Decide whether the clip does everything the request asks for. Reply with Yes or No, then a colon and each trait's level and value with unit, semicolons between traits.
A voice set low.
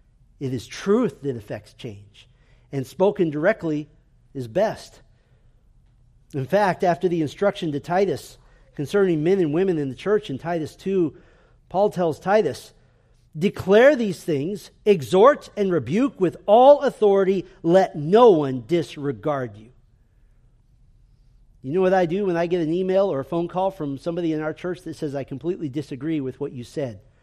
No: medium, 155 Hz